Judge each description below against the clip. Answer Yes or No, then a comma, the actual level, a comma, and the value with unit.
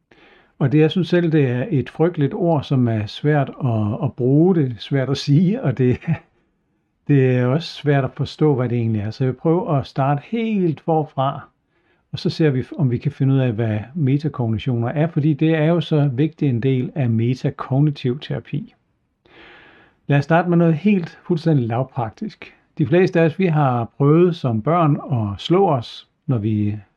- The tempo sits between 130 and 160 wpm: No, average, 190 wpm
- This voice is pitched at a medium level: Yes, medium, 145 Hz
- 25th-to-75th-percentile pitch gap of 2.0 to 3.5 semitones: No, average, 4.2 semitones